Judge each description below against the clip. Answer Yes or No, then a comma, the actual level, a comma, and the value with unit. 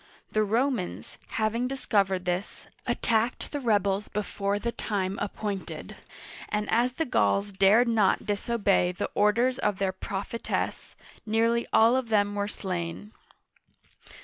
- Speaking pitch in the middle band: No, high, 210 Hz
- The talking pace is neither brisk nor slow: No, slow, 125 wpm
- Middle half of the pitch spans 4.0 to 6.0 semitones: No, average, 2.9 semitones